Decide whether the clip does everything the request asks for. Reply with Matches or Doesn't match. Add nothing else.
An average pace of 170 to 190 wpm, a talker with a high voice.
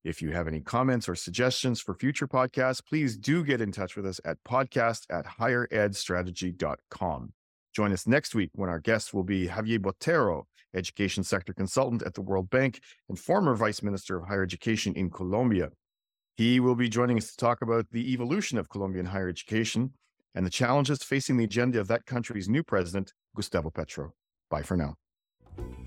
Doesn't match